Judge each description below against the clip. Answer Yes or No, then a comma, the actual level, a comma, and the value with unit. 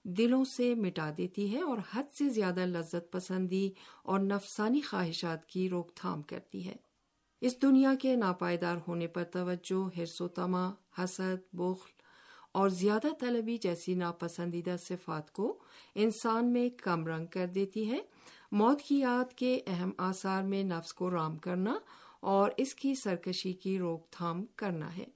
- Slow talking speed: No, average, 150 wpm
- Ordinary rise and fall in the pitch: Yes, average, 5.0 semitones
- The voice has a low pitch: No, high, 190 Hz